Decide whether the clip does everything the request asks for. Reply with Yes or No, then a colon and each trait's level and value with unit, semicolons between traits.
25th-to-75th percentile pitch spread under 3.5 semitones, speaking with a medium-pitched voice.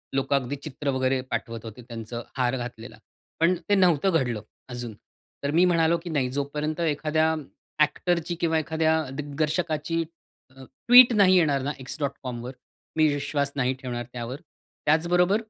No: average, 4.1 semitones; medium, 145 Hz